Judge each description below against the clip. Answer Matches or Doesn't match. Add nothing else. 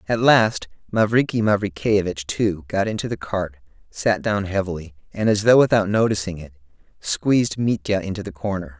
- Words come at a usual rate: Matches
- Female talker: Doesn't match